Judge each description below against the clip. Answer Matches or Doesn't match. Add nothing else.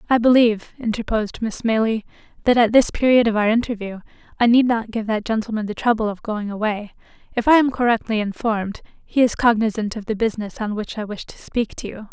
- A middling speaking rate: Doesn't match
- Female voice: Matches